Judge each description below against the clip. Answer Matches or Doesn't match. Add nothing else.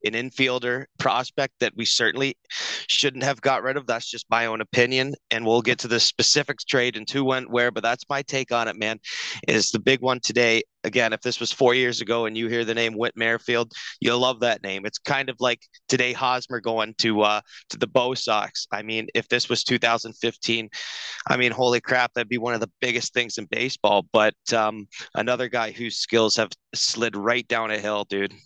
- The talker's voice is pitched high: Doesn't match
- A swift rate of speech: Matches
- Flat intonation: Matches